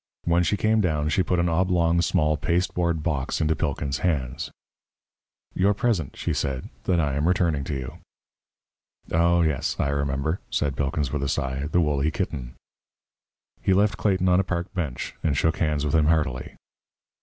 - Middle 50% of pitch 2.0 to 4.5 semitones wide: Yes, average, 3.8 semitones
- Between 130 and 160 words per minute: No, average, 170 wpm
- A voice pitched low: Yes, very low, 80 Hz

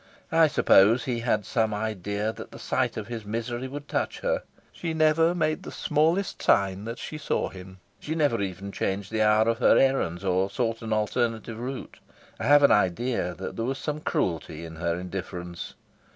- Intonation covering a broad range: Yes, wide, 5.8 semitones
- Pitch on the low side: Yes, low, 110 Hz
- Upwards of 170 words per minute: Yes, average, 190 wpm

